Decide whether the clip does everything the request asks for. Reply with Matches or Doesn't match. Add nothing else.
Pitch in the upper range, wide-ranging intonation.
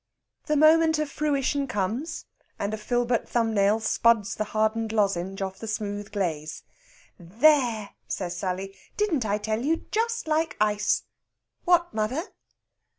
Matches